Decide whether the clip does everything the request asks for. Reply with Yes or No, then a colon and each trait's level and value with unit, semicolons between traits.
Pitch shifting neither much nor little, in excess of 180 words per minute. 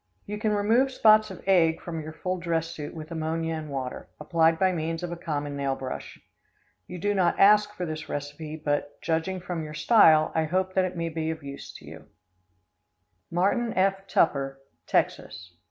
Yes: average, 3.3 semitones; average, 190 wpm